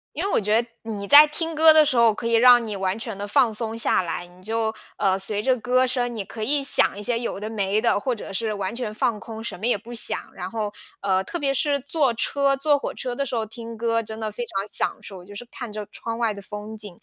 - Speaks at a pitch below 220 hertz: No, high, 225 Hz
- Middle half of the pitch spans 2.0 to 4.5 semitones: Yes, average, 3.1 semitones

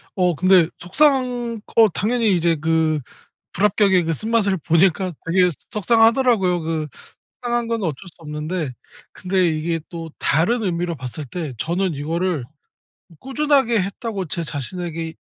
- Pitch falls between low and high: Yes, medium, 180 Hz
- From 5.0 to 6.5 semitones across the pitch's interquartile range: Yes, average, 5.3 semitones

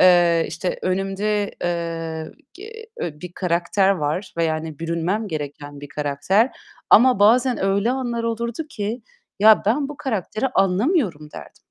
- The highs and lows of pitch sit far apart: Yes, wide, 5.9 semitones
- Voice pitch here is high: Yes, high, 195 Hz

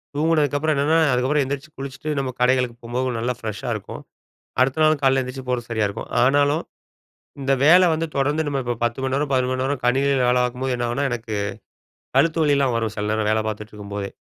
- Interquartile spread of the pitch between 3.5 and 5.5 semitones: No, average, 3.1 semitones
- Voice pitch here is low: Yes, low, 130 Hz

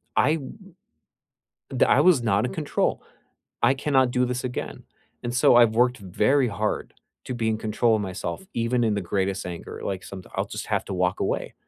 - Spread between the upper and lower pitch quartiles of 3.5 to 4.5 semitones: Yes, average, 4.2 semitones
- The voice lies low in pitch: Yes, low, 115 Hz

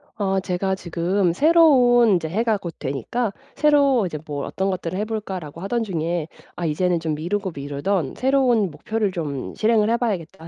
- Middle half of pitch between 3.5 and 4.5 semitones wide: No, average, 5.1 semitones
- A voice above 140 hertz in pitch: Yes, high, 190 Hz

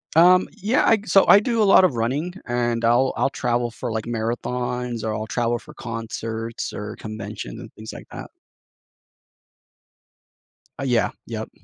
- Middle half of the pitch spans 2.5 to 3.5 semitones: No, average, 4.8 semitones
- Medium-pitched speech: No, low, 120 Hz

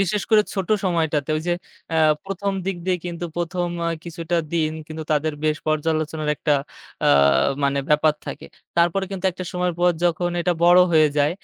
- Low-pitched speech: No, medium, 170 Hz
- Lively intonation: No, narrow, 2.5 semitones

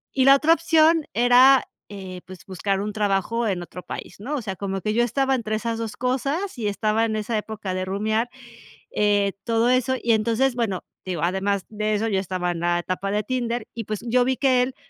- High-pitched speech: Yes, high, 220 Hz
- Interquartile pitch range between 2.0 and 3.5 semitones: No, average, 4.0 semitones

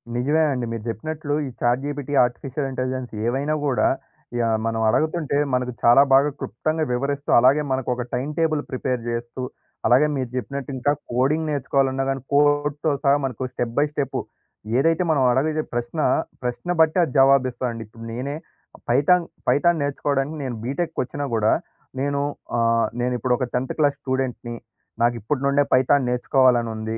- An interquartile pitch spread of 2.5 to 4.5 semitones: Yes, average, 2.9 semitones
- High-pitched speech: No, low, 135 Hz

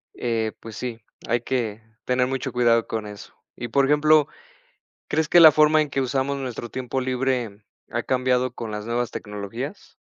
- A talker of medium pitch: No, low, 125 Hz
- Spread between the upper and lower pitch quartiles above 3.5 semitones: No, average, 2.7 semitones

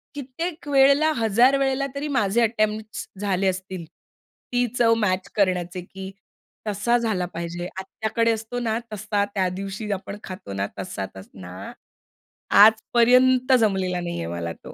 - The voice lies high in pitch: Yes, high, 210 Hz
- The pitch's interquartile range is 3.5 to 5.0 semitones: Yes, average, 4.5 semitones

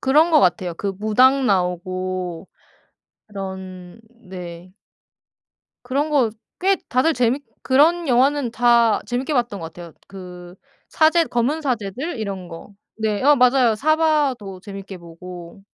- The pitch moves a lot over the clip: Yes, wide, 6.7 semitones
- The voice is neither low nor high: No, high, 220 Hz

